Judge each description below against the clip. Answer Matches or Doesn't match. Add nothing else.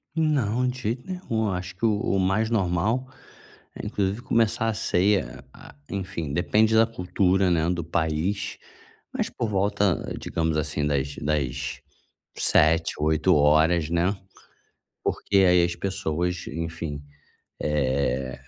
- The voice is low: Matches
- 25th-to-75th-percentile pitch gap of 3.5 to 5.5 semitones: Matches